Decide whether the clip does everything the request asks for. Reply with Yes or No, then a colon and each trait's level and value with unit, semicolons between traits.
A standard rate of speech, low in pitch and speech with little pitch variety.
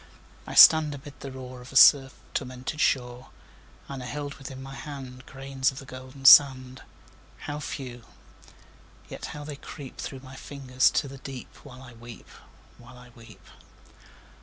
Yes: average, 160 wpm; low, 130 Hz; narrow, 1.5 semitones